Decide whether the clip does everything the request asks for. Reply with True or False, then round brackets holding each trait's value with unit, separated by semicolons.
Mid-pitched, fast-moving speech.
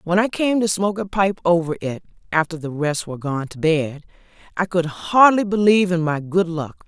True (175 Hz; 210 wpm)